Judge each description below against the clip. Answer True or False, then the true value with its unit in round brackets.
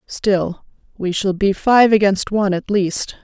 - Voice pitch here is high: True (200 Hz)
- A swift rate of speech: False (165 wpm)